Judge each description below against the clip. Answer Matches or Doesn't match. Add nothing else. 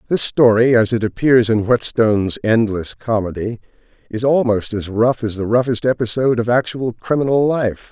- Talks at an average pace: Matches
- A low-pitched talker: Matches